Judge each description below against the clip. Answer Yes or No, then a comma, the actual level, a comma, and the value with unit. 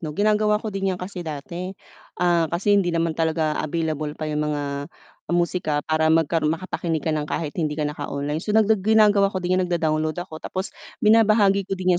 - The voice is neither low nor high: Yes, medium, 170 Hz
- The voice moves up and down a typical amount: Yes, average, 3.7 semitones